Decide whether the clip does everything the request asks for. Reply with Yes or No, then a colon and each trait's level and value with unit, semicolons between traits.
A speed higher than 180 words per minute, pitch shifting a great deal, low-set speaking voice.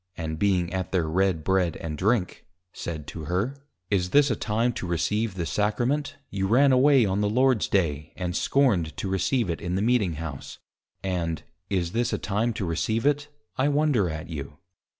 Yes: average, 190 wpm; wide, 5.9 semitones; very low, 95 Hz